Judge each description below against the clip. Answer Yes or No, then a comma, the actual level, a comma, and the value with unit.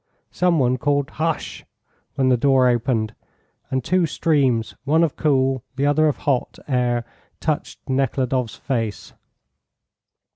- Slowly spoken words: Yes, slow, 125 wpm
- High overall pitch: No, low, 135 Hz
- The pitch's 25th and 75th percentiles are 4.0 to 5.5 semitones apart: No, average, 2.9 semitones